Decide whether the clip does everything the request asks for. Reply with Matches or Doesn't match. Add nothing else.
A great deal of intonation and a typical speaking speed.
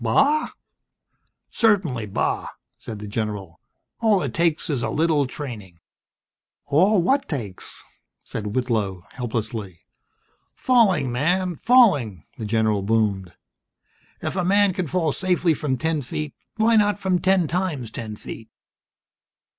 Doesn't match